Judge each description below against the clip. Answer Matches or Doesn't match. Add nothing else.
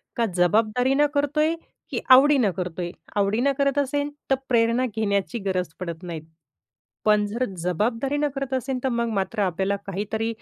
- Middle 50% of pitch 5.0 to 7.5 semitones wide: Matches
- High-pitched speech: Matches